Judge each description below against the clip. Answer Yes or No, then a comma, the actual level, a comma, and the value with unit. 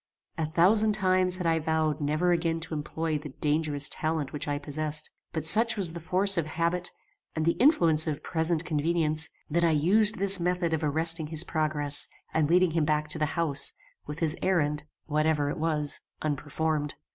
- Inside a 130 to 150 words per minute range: No, average, 180 wpm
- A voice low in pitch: No, medium, 160 Hz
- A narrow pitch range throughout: Yes, narrow, 2.2 semitones